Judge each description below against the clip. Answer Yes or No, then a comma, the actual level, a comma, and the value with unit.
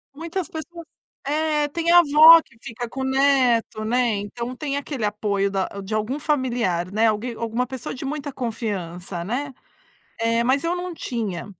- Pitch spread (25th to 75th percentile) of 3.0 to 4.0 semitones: No, average, 5.2 semitones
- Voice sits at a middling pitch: No, very high, 250 Hz